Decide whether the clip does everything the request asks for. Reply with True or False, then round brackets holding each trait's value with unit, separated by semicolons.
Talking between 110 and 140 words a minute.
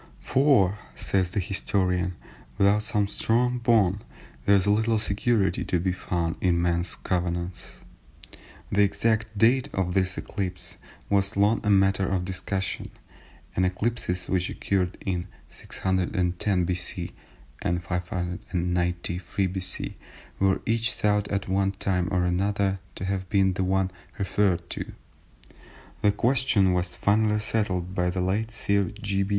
True (135 wpm)